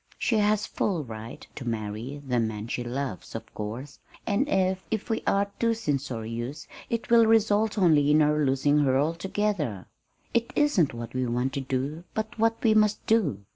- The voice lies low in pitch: No, medium, 150 Hz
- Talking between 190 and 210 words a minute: No, average, 175 wpm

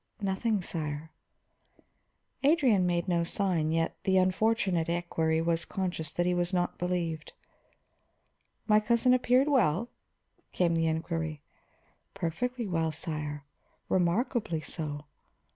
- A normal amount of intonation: Yes, average, 4.0 semitones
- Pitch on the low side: No, medium, 175 Hz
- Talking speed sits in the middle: No, slow, 110 wpm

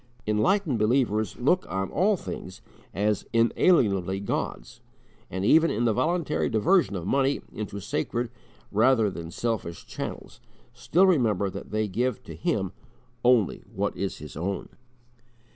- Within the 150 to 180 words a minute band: No, slow, 135 wpm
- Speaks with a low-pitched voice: Yes, low, 110 Hz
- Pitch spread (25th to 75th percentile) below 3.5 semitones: No, wide, 5.5 semitones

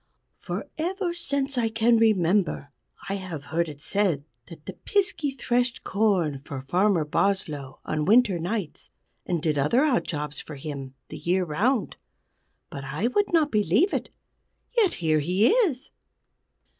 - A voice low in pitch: No, high, 190 Hz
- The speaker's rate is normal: Yes, average, 150 wpm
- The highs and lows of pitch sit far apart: Yes, wide, 8.2 semitones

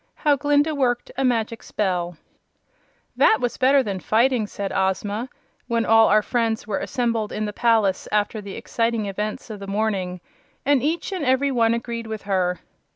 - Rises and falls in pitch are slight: No, average, 3.5 semitones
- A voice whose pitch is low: No, high, 225 Hz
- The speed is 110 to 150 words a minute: No, average, 170 wpm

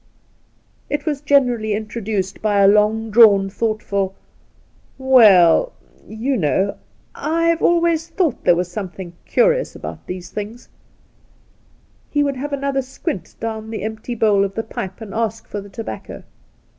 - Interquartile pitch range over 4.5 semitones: Yes, wide, 5.5 semitones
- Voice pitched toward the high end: Yes, high, 220 Hz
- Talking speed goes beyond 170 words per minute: No, average, 145 wpm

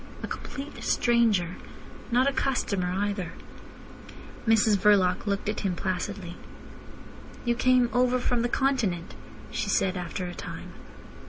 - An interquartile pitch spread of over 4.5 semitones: Yes, average, 4.9 semitones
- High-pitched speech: Yes, high, 205 Hz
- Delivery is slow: Yes, slow, 130 wpm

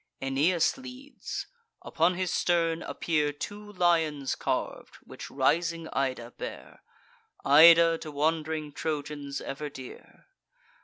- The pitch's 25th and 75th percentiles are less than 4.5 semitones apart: Yes, average, 2.8 semitones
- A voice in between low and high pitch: Yes, medium, 160 Hz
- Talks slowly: Yes, slow, 105 wpm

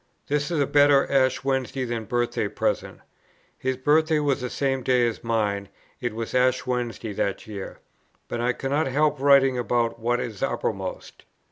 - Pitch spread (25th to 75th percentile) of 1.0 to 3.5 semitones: Yes, average, 2.9 semitones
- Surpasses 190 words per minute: No, average, 165 wpm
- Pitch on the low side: Yes, low, 125 Hz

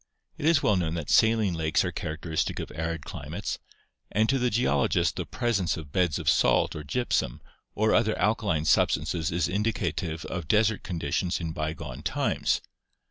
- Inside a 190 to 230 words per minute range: No, average, 165 wpm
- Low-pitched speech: Yes, very low, 90 Hz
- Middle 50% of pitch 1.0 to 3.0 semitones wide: No, wide, 5.4 semitones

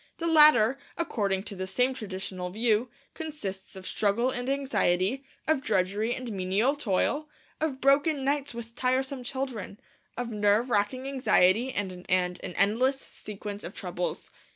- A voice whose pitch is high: Yes, high, 230 Hz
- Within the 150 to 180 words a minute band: No, average, 140 wpm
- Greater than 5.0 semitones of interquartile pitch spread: Yes, wide, 5.5 semitones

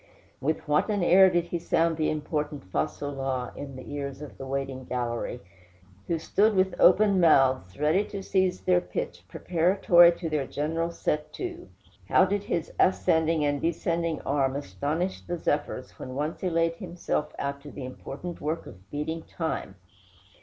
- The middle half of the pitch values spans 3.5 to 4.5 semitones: Yes, average, 3.8 semitones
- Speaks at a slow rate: No, average, 170 wpm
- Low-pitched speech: No, medium, 160 Hz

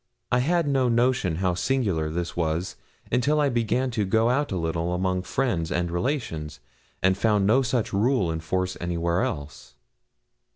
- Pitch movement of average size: No, wide, 6.5 semitones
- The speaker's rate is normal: Yes, average, 165 wpm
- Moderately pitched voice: No, very low, 95 Hz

